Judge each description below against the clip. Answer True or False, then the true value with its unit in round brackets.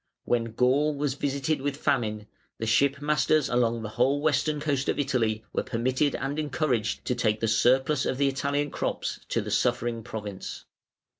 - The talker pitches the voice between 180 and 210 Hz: False (130 Hz)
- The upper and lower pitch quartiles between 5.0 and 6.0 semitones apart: False (3.8 semitones)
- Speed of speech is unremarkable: True (170 wpm)